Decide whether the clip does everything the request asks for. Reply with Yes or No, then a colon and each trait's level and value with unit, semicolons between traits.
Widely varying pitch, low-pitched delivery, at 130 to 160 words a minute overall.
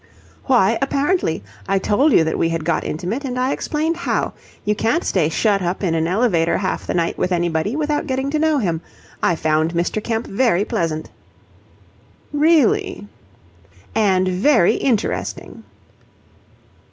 No: wide, 8.2 semitones; high, 205 Hz; average, 150 wpm